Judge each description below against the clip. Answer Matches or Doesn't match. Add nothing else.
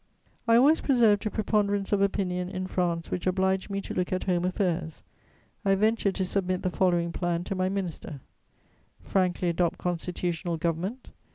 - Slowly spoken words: Doesn't match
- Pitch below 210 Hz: Matches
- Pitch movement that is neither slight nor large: Doesn't match